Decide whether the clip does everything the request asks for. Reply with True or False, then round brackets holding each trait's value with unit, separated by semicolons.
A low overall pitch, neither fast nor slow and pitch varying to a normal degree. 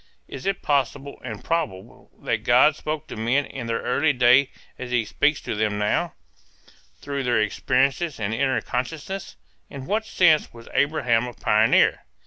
True (130 Hz; 160 wpm; 4.2 semitones)